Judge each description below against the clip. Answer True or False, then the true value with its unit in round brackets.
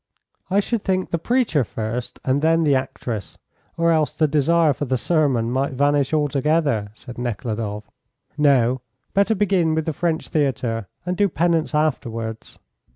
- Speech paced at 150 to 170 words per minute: True (155 wpm)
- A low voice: False (145 Hz)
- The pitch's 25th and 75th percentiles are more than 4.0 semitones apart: True (5.2 semitones)